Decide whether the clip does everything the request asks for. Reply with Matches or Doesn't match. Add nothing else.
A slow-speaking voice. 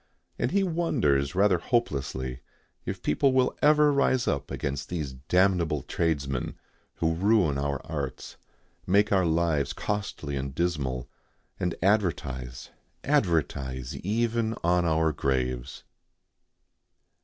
Matches